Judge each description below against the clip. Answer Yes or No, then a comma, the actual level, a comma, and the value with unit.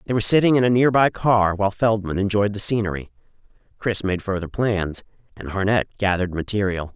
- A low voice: Yes, low, 100 Hz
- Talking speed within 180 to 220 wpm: No, average, 170 wpm